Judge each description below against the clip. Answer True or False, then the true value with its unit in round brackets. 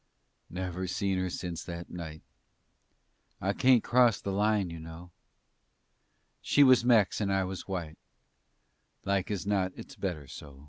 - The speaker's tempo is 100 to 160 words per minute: True (145 wpm)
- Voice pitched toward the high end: False (95 Hz)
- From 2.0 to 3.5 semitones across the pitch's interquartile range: True (2.8 semitones)